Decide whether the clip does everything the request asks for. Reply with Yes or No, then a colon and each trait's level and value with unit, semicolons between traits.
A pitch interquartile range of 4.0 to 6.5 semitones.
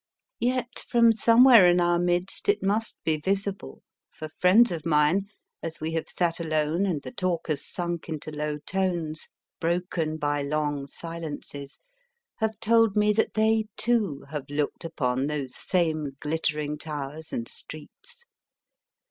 Yes: average, 4.8 semitones